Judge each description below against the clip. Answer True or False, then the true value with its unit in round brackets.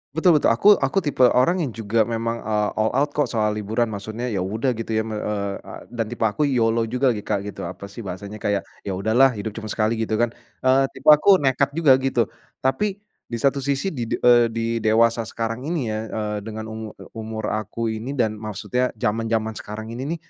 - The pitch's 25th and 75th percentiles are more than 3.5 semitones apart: False (3.2 semitones)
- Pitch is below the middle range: True (115 Hz)